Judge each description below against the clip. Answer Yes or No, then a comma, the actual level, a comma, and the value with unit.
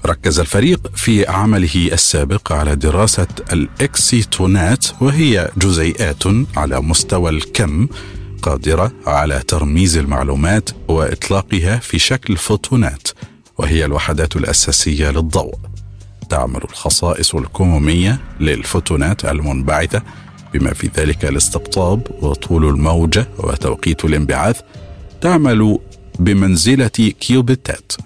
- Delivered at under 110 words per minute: Yes, average, 90 wpm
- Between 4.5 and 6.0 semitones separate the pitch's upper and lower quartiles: Yes, average, 4.9 semitones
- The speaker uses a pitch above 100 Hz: No, very low, 95 Hz